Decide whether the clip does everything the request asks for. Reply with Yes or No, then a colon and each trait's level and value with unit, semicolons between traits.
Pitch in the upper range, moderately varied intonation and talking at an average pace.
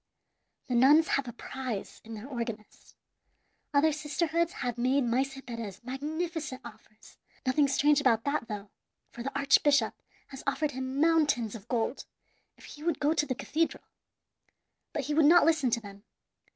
Yes: very high, 270 Hz; average, 4.0 semitones; average, 165 wpm